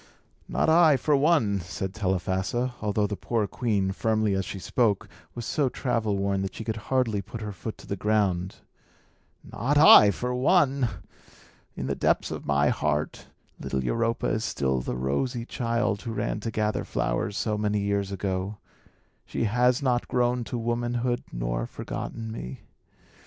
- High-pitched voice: No, low, 110 Hz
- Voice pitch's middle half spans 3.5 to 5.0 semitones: Yes, average, 3.9 semitones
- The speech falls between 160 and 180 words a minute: Yes, average, 165 wpm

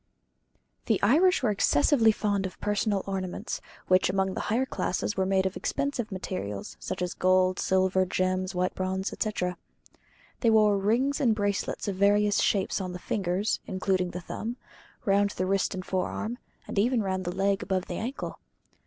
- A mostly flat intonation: Yes, narrow, 2.3 semitones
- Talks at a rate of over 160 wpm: Yes, average, 170 wpm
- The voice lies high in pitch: Yes, high, 195 Hz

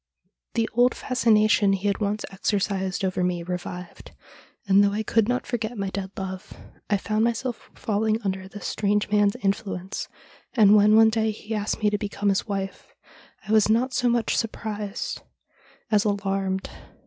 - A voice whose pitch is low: No, high, 205 Hz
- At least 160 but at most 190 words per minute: Yes, average, 165 wpm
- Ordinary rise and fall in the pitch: No, narrow, 2.1 semitones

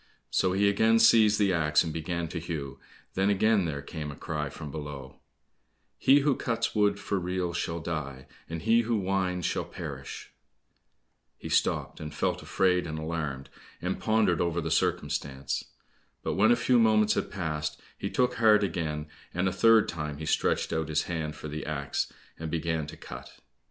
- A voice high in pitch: No, very low, 85 Hz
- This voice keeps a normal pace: Yes, average, 180 wpm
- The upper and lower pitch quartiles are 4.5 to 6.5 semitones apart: Yes, average, 4.9 semitones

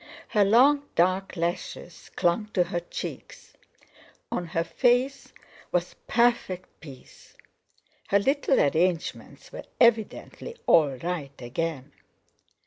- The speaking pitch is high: No, medium, 180 Hz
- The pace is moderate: No, slow, 100 wpm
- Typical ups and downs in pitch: No, wide, 6.1 semitones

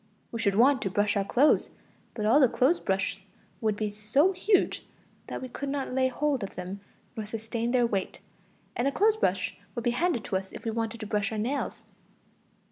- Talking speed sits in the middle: No, fast, 210 wpm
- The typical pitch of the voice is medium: No, high, 230 Hz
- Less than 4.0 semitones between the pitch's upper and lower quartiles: No, average, 4.5 semitones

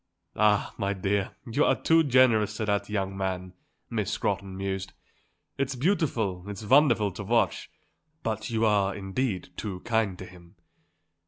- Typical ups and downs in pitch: Yes, average, 3.2 semitones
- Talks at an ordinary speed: Yes, average, 150 wpm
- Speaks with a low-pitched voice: Yes, low, 105 Hz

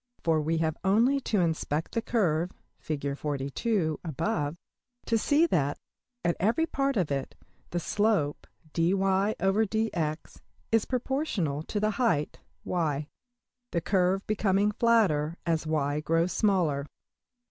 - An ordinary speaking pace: No, slow, 110 wpm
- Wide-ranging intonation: Yes, wide, 5.7 semitones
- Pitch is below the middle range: No, medium, 180 Hz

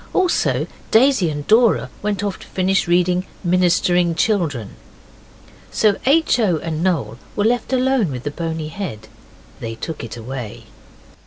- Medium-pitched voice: Yes, medium, 180 Hz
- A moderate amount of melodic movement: No, wide, 6.1 semitones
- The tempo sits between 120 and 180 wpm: Yes, average, 140 wpm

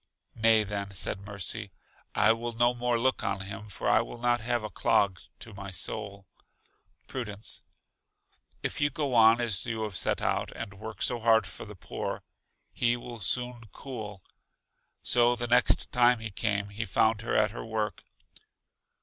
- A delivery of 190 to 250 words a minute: No, average, 170 wpm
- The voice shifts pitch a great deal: No, average, 2.9 semitones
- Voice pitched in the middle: No, low, 110 Hz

